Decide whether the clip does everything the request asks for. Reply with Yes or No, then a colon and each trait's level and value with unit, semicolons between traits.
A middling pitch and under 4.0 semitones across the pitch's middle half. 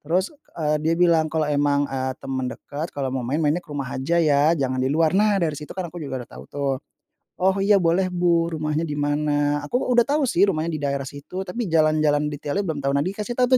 Yes: medium, 155 Hz; average, 3.6 semitones